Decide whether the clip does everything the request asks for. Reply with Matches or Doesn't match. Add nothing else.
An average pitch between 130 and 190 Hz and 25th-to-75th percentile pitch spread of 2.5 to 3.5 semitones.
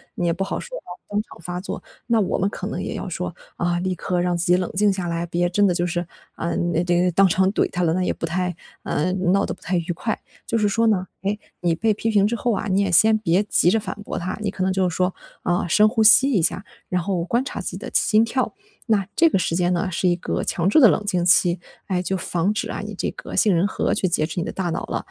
Matches